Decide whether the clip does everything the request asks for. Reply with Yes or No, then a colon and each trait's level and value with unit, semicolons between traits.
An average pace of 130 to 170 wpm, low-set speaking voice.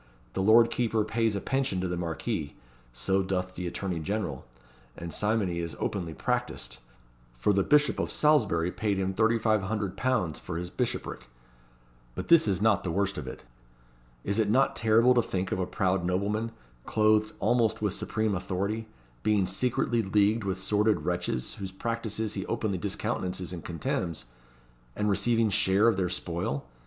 Yes: average, 160 wpm; low, 100 Hz